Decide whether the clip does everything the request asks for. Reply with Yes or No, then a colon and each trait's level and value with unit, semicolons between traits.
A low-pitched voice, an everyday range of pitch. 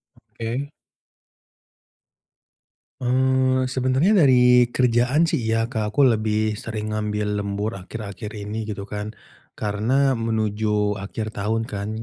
Yes: low, 110 Hz; average, 3.1 semitones